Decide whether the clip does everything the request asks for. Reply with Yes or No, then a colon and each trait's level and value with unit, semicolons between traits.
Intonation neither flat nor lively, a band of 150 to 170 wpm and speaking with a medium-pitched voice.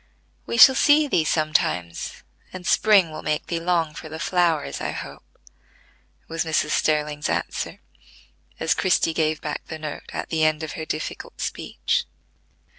No: narrow, 2.1 semitones; average, 155 wpm; medium, 160 Hz